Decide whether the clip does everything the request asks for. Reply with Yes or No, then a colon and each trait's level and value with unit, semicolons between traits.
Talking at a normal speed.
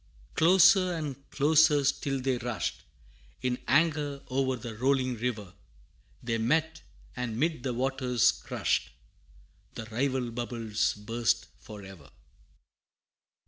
No: slow, 110 wpm